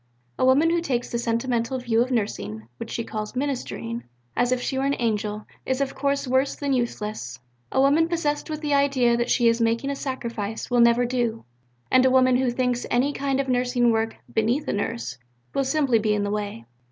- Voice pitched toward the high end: Yes, high, 245 Hz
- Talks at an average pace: No, fast, 210 wpm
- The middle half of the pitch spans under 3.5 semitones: Yes, average, 3.0 semitones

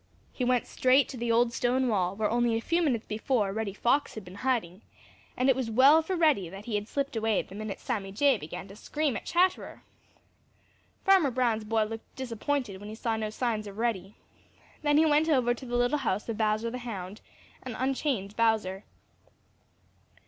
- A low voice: No, high, 230 Hz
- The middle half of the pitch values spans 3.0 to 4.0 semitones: Yes, average, 3.7 semitones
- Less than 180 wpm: No, average, 195 wpm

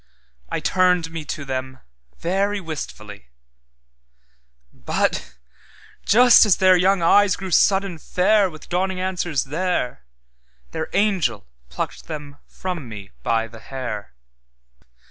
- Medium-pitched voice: Yes, medium, 145 Hz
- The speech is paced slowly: Yes, slow, 105 wpm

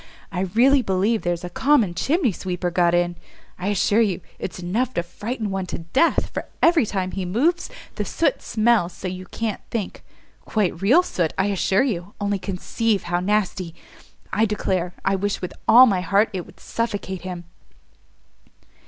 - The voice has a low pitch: No, high, 195 Hz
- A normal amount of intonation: Yes, average, 4.0 semitones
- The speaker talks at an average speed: Yes, average, 170 wpm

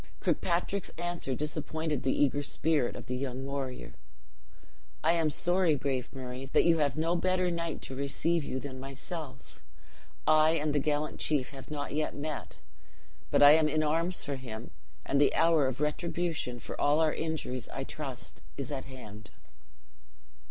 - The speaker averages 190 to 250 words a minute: No, average, 165 wpm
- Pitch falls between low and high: Yes, medium, 145 Hz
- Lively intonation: No, average, 3.3 semitones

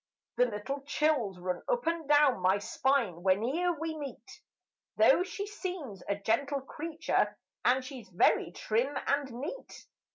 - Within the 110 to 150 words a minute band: Yes, average, 140 wpm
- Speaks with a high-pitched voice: Yes, very high, 270 Hz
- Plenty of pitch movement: Yes, wide, 6.8 semitones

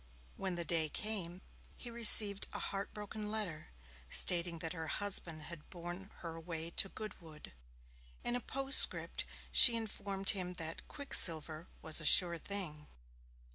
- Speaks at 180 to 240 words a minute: No, average, 140 wpm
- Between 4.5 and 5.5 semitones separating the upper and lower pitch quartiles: No, average, 3.9 semitones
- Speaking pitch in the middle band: Yes, medium, 180 Hz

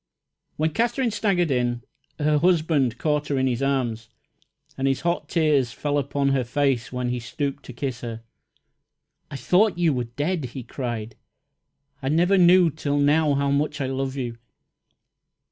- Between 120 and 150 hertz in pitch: Yes, medium, 140 Hz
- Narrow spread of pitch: No, average, 4.0 semitones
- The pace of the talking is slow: No, average, 160 wpm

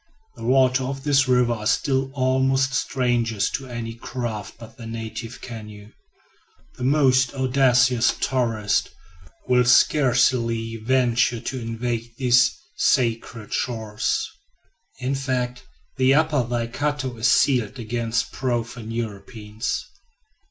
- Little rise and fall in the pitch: Yes, narrow, 2.3 semitones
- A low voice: Yes, low, 125 Hz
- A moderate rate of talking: No, slow, 110 wpm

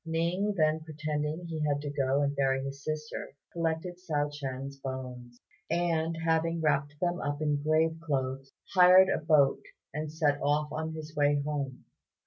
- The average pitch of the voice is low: No, medium, 150 Hz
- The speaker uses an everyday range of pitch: No, narrow, 2.3 semitones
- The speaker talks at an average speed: Yes, average, 160 wpm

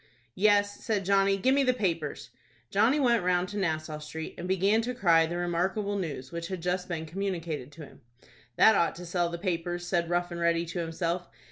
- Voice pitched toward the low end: No, medium, 175 Hz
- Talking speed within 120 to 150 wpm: No, fast, 205 wpm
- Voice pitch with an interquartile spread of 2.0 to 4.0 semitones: Yes, average, 2.9 semitones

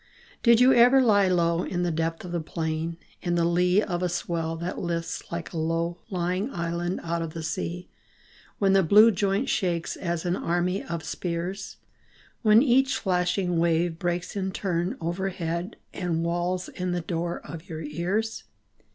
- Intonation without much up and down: Yes, narrow, 2.2 semitones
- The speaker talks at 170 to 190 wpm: Yes, average, 175 wpm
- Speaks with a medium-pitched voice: Yes, medium, 175 Hz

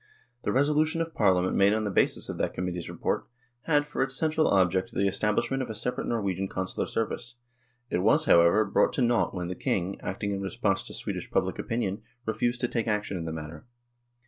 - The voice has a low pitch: Yes, low, 105 Hz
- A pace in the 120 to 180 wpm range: No, fast, 205 wpm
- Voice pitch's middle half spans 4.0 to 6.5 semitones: Yes, average, 4.6 semitones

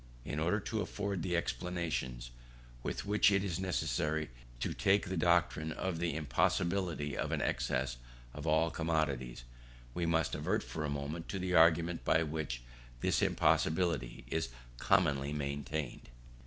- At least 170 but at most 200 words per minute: No, average, 145 wpm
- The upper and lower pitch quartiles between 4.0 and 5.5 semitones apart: No, average, 3.3 semitones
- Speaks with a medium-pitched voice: No, very low, 80 Hz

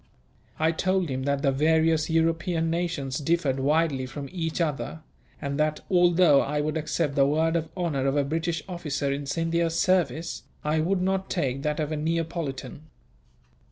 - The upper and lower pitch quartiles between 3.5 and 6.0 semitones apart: No, average, 2.9 semitones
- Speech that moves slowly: No, average, 165 wpm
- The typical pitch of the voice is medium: Yes, medium, 160 Hz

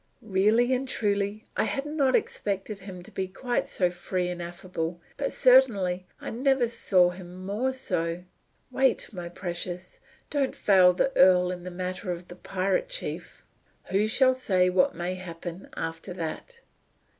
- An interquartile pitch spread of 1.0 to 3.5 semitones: No, average, 5.2 semitones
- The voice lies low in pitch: No, medium, 185 Hz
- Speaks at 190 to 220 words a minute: No, average, 155 wpm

